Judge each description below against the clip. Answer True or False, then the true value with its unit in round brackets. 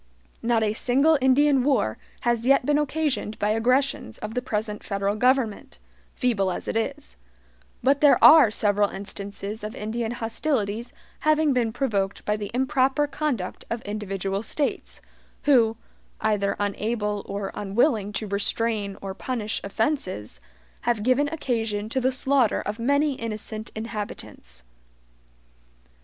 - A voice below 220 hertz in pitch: False (225 Hz)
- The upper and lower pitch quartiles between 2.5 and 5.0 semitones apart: True (4.2 semitones)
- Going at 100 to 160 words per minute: True (135 wpm)